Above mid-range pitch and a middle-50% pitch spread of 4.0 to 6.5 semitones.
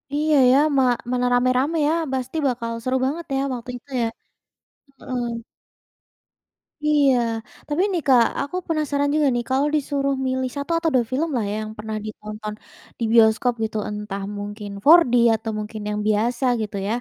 Yes: very high, 255 Hz; average, 4.5 semitones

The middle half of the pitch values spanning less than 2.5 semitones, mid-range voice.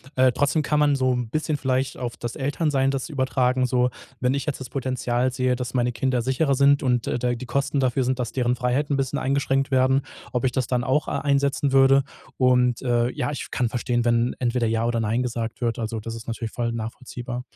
No: narrow, 2.0 semitones; low, 125 Hz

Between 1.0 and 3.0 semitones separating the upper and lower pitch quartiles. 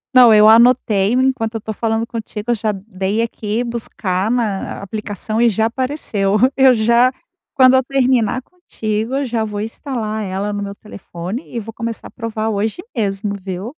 Yes: narrow, 2.6 semitones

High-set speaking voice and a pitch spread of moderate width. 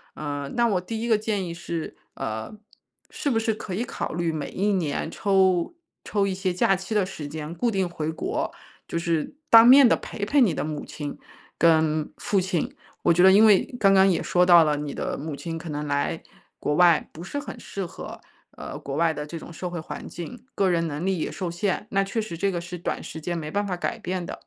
No: medium, 175 Hz; average, 3.7 semitones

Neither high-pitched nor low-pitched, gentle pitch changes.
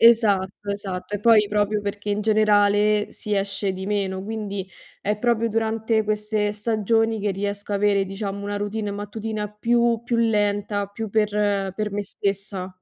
No: high, 210 Hz; narrow, 1.2 semitones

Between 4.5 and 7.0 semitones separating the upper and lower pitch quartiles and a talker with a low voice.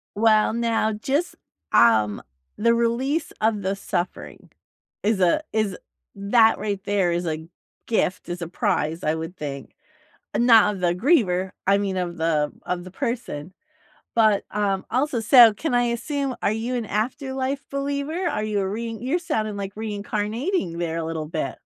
No: average, 4.9 semitones; high, 210 Hz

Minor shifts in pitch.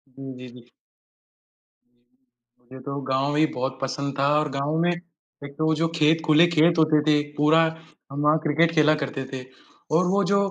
No: average, 3.2 semitones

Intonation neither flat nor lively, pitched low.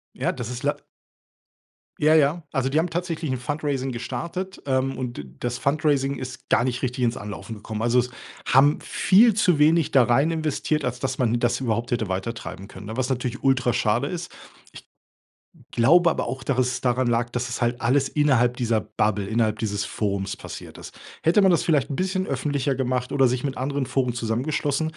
Yes: average, 3.4 semitones; low, 130 Hz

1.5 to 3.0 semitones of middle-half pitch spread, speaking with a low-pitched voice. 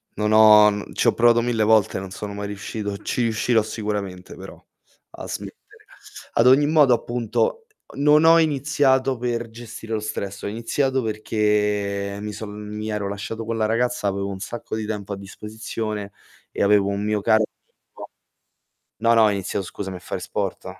Yes: narrow, 2.5 semitones; low, 110 Hz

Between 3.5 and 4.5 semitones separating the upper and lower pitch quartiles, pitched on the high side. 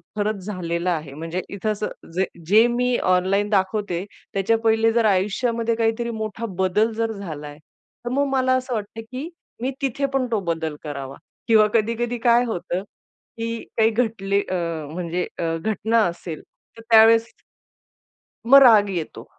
Yes: average, 4.1 semitones; high, 215 Hz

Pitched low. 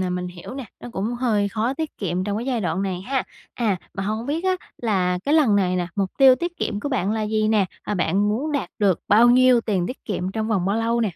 No: high, 215 Hz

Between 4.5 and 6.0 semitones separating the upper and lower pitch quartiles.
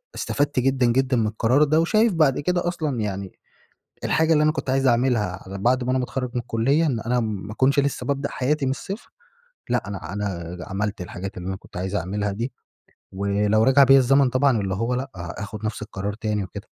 Yes: average, 5.1 semitones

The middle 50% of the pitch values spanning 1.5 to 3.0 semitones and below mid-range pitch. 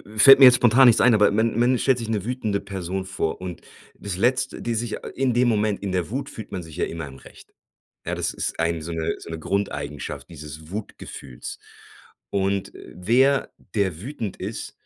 No: wide, 5.5 semitones; low, 100 Hz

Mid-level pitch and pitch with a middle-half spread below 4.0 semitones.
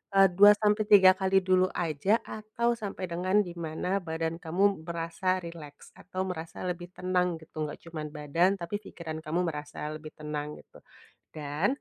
Yes: medium, 175 Hz; average, 3.3 semitones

